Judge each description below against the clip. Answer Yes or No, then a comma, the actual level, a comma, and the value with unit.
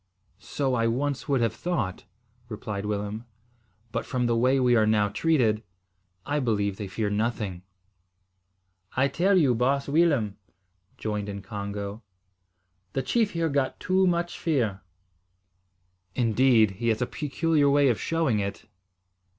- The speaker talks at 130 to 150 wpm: Yes, average, 140 wpm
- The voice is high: No, low, 120 Hz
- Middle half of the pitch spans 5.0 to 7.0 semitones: Yes, average, 5.3 semitones